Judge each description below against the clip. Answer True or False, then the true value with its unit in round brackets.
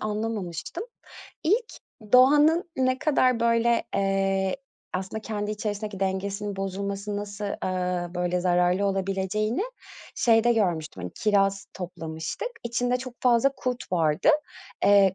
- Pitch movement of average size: True (3.9 semitones)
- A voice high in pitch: True (200 Hz)